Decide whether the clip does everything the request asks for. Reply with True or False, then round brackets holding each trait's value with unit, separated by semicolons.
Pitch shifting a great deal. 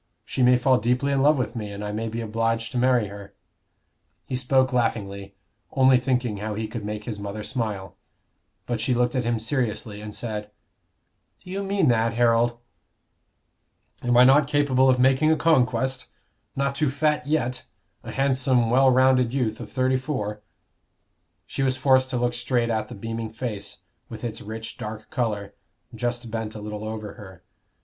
False (3.2 semitones)